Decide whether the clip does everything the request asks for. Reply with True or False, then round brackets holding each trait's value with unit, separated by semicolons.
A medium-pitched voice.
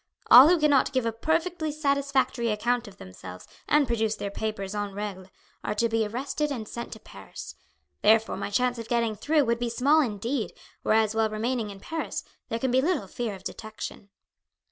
False (230 Hz)